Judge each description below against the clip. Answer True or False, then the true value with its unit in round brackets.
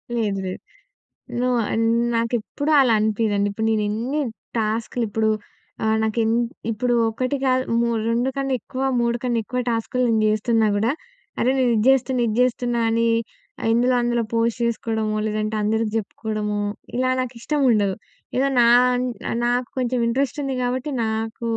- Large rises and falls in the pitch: False (2.4 semitones)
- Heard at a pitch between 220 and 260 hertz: True (230 Hz)